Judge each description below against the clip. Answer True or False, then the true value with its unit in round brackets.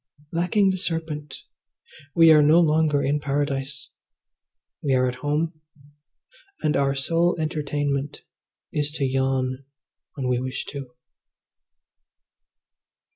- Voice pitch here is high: False (145 Hz)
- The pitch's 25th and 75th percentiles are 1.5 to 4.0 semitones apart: True (2.8 semitones)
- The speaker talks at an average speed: False (110 wpm)